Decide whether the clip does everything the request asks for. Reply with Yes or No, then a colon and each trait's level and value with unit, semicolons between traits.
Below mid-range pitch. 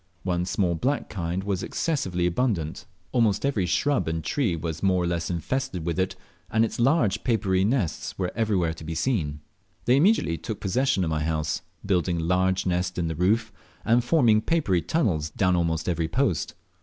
Yes: very low, 95 Hz